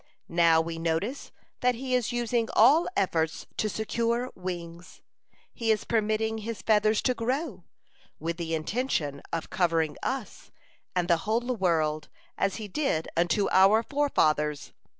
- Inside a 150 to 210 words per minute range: No, average, 140 wpm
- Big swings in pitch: Yes, wide, 5.9 semitones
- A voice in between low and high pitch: No, high, 210 Hz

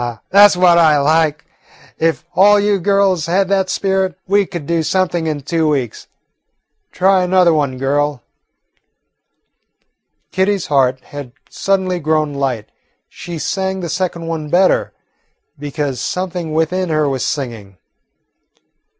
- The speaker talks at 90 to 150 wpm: Yes, slow, 135 wpm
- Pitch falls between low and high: Yes, medium, 165 Hz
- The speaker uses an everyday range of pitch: Yes, average, 4.4 semitones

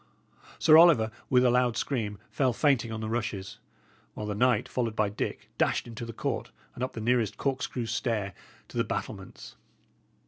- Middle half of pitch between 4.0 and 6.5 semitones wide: No, narrow, 2.6 semitones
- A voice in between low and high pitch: No, low, 115 Hz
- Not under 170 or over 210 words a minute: Yes, average, 175 wpm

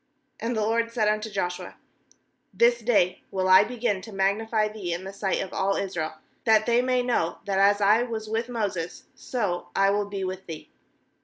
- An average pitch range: Yes, average, 3.0 semitones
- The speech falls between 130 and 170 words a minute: No, average, 190 wpm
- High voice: Yes, high, 205 Hz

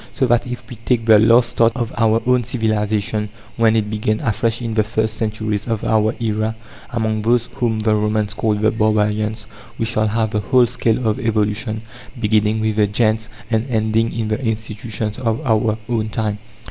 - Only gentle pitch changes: Yes, narrow, 1.2 semitones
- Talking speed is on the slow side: No, average, 185 wpm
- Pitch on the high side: No, low, 110 Hz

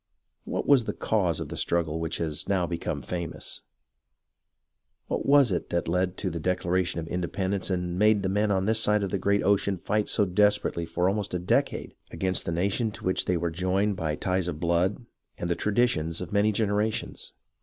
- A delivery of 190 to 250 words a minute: Yes, average, 200 wpm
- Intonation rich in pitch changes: No, average, 3.0 semitones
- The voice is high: No, very low, 95 Hz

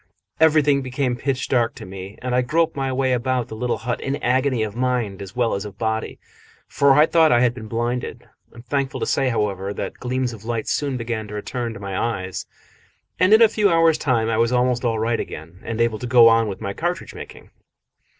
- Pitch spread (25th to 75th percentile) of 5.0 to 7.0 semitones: No, average, 3.2 semitones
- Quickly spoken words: Yes, fast, 230 wpm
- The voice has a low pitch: Yes, low, 120 Hz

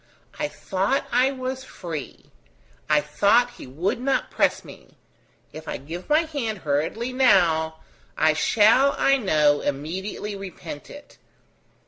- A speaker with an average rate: No, slow, 130 wpm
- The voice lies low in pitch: No, high, 200 Hz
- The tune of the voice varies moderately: No, wide, 8.5 semitones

